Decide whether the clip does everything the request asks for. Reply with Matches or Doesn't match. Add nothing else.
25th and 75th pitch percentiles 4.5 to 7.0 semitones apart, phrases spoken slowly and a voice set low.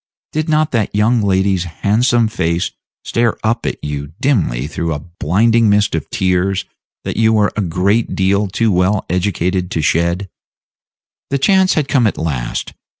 Doesn't match